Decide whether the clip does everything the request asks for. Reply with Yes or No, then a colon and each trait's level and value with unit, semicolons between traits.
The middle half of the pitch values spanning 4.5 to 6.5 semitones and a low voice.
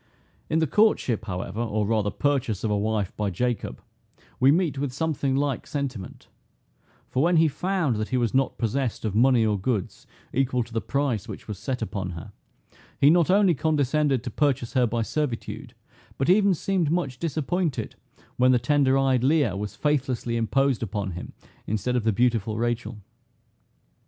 Yes: average, 4.8 semitones; low, 125 Hz